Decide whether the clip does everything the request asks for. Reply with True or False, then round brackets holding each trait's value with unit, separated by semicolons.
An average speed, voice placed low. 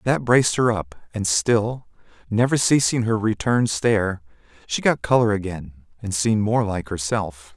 True (145 wpm; 110 Hz)